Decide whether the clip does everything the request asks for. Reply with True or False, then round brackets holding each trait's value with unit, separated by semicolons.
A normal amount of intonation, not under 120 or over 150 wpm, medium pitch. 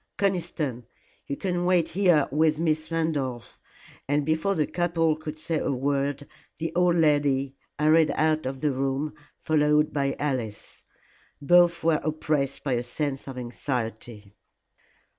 True (3.0 semitones; 140 wpm; 150 Hz)